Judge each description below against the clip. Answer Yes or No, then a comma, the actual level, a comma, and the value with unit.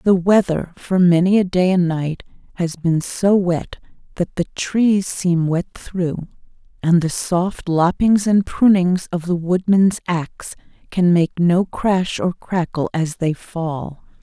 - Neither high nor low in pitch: Yes, medium, 175 Hz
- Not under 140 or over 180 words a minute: Yes, average, 155 wpm